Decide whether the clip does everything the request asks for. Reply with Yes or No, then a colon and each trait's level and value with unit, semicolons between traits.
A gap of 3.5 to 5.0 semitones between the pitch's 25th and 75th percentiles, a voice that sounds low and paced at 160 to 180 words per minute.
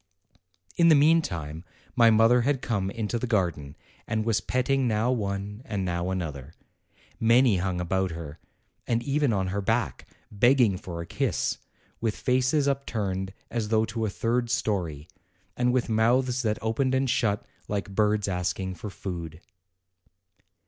No: average, 4.6 semitones; low, 110 Hz; average, 150 wpm